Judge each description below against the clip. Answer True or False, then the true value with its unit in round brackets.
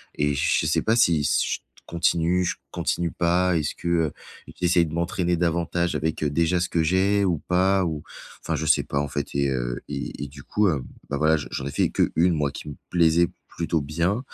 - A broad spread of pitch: False (2.8 semitones)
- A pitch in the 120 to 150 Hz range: False (85 Hz)